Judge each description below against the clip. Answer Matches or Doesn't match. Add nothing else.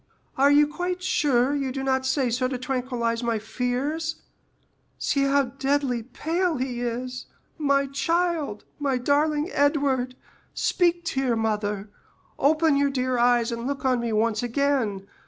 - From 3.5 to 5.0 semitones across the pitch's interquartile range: Doesn't match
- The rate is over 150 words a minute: Doesn't match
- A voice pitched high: Matches